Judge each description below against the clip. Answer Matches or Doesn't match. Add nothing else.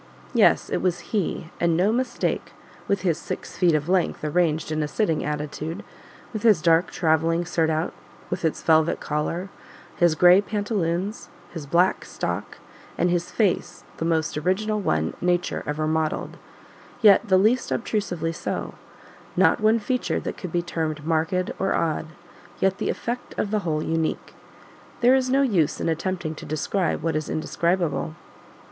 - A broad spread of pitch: Doesn't match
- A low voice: Doesn't match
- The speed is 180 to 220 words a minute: Doesn't match